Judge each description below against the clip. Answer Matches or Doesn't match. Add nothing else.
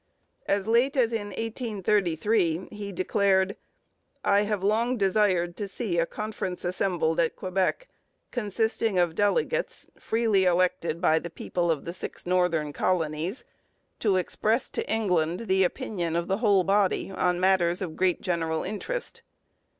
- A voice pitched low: Doesn't match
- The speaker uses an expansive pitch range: Doesn't match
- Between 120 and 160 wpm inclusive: Matches